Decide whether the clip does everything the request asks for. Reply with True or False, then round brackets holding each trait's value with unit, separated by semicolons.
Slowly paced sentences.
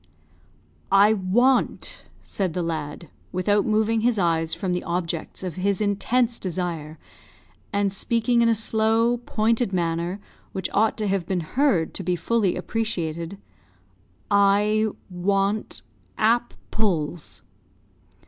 True (120 wpm)